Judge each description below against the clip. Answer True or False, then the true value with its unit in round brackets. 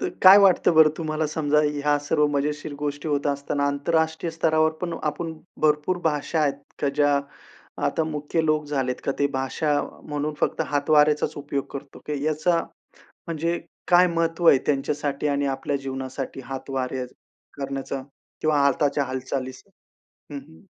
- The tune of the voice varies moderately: False (2.1 semitones)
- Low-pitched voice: False (150 Hz)